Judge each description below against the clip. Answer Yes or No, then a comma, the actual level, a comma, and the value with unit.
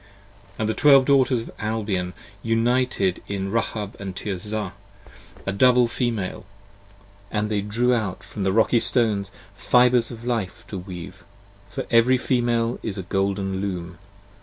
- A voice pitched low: Yes, low, 110 Hz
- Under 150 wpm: Yes, average, 140 wpm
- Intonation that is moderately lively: Yes, average, 3.7 semitones